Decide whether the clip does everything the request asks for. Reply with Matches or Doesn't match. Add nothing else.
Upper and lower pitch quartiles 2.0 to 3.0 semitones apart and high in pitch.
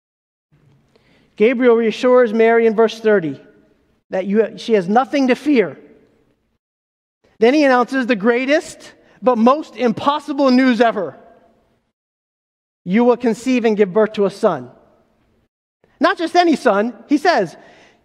Doesn't match